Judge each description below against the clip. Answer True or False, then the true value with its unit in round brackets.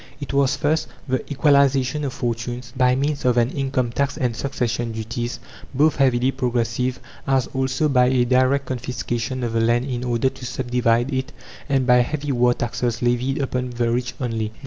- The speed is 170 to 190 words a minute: True (180 wpm)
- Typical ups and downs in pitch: False (1.9 semitones)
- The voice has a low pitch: True (125 Hz)